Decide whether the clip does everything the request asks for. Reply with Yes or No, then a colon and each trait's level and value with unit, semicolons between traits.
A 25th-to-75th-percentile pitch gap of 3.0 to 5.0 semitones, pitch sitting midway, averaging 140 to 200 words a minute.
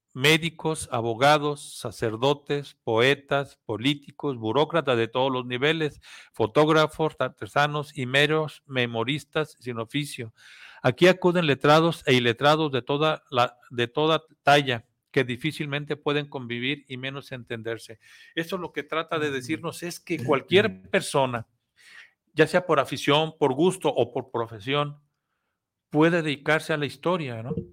No: average, 3.5 semitones; medium, 145 Hz; average, 130 wpm